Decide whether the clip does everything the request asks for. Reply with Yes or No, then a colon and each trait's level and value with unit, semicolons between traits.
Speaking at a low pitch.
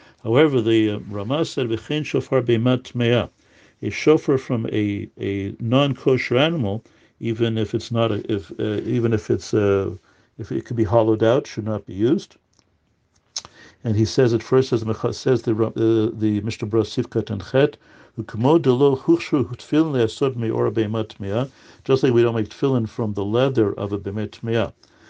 Yes: low, 115 Hz